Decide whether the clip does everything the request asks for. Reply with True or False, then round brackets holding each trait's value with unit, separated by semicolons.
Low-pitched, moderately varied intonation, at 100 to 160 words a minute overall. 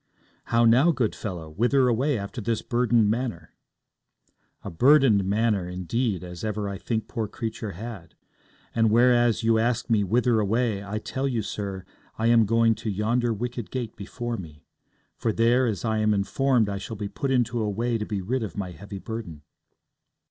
False (110 Hz; 3.1 semitones; 180 wpm)